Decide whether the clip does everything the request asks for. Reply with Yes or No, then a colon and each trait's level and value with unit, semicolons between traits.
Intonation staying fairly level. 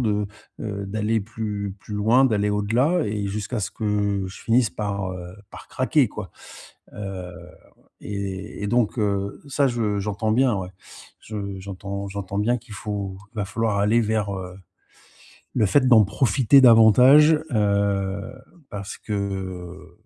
Yes: narrow, 2.2 semitones